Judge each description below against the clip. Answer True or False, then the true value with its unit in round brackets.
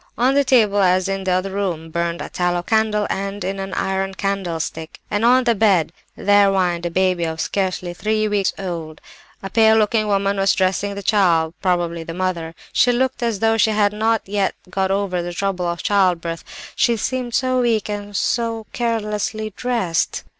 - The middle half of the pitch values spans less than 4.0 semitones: True (3.3 semitones)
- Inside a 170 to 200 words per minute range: True (190 wpm)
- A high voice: True (195 Hz)